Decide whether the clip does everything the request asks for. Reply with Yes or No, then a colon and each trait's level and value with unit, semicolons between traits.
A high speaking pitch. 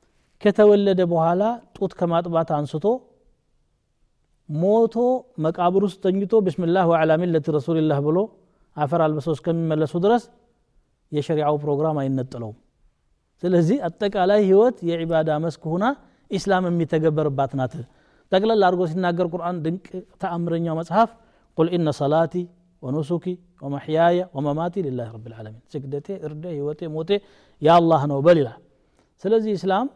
No: medium, 170 Hz